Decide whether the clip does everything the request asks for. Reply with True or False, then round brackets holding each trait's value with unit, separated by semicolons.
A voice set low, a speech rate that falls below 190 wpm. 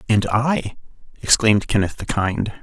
True (110 Hz; 135 wpm)